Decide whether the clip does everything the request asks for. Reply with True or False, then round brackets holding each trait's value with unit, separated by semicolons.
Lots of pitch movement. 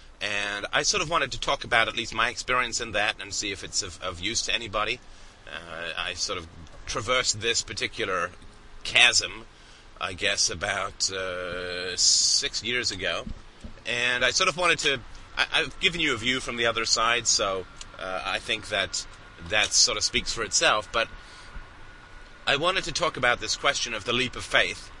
False (4.2 semitones)